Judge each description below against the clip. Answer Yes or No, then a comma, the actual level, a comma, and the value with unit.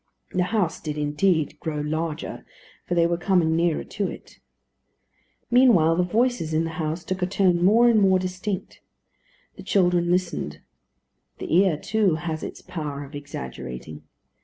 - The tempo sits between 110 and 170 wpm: Yes, average, 155 wpm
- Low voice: No, medium, 175 Hz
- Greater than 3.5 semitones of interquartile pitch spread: No, average, 3.1 semitones